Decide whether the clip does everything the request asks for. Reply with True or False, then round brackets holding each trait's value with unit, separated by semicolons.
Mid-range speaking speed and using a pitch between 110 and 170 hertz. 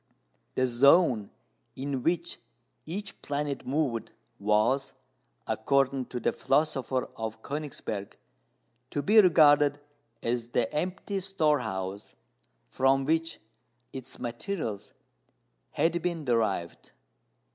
False (95 wpm; 135 Hz)